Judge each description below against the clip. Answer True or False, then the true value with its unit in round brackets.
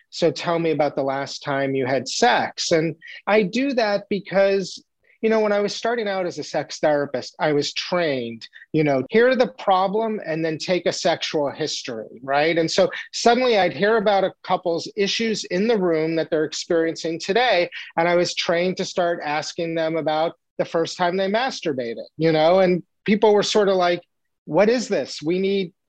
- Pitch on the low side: False (175 Hz)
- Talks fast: False (195 wpm)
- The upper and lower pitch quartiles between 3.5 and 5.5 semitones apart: True (4.0 semitones)